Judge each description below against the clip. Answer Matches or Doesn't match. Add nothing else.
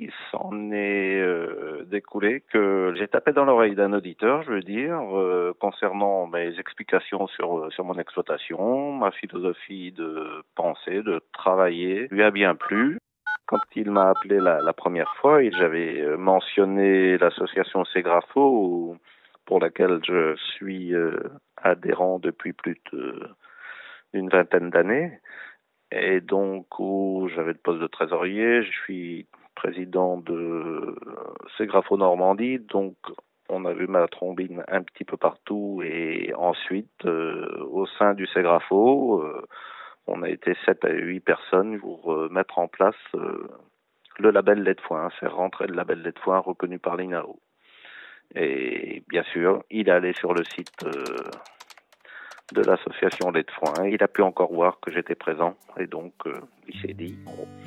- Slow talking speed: Doesn't match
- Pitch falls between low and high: Doesn't match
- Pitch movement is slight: Matches